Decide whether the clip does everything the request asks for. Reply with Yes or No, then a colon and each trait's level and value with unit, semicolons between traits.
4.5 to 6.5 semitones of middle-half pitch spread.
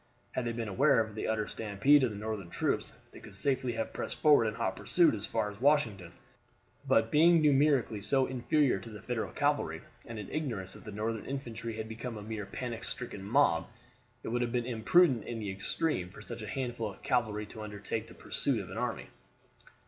No: average, 3.6 semitones